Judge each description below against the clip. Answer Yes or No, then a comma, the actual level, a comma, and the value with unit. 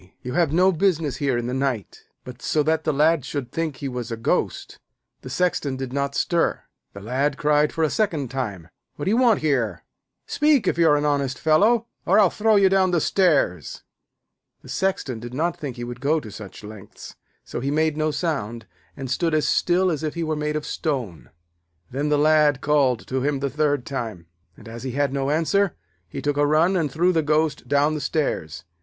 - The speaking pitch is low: No, medium, 145 Hz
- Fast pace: Yes, fast, 215 wpm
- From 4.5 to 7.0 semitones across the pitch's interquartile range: No, average, 4.1 semitones